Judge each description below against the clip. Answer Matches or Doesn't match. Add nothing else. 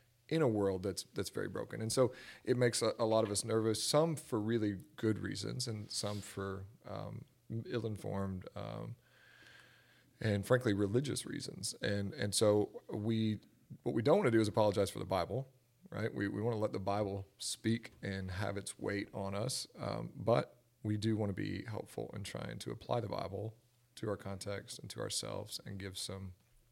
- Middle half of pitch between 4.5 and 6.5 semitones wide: Doesn't match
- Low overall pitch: Matches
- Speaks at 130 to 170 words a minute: Doesn't match